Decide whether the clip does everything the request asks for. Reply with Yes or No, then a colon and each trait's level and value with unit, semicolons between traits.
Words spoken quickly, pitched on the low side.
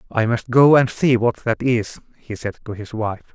Yes: fast, 235 wpm; low, 115 Hz